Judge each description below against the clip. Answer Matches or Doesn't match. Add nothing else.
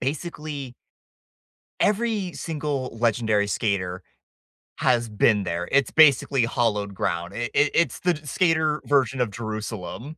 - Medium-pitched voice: Doesn't match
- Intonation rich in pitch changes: Matches